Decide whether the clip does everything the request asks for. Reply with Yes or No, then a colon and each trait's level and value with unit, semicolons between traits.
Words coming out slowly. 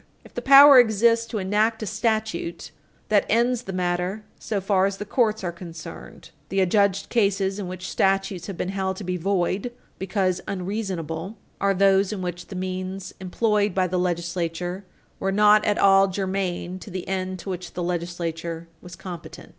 No: average, 175 wpm